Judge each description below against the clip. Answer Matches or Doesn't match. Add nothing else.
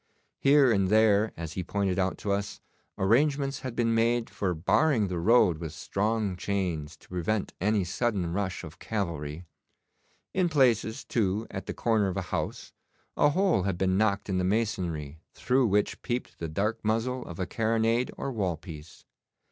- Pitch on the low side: Matches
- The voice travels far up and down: Doesn't match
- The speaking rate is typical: Matches